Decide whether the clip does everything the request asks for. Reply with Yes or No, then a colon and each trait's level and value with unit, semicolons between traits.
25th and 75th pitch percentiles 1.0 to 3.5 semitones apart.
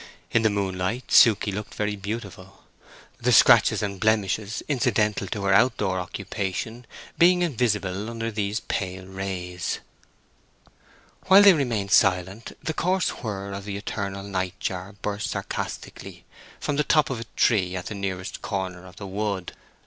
Yes: average, 3.1 semitones